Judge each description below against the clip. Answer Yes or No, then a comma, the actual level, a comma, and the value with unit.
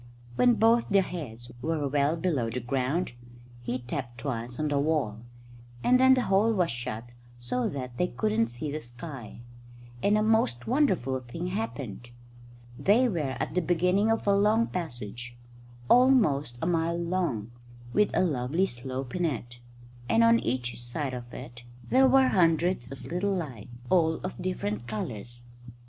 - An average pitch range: No, wide, 7.4 semitones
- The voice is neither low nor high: Yes, medium, 150 Hz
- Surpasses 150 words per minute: Yes, average, 160 wpm